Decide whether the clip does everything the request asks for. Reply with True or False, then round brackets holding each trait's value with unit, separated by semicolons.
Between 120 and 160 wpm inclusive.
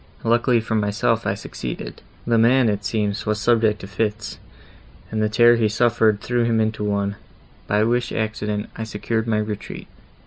False (170 wpm)